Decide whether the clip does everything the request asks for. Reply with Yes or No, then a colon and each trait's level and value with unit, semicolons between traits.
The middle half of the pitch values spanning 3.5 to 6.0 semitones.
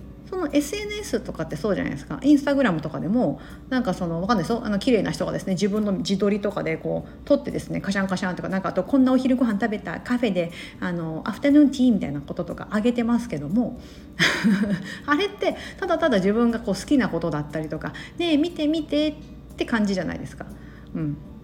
No: wide, 7.2 semitones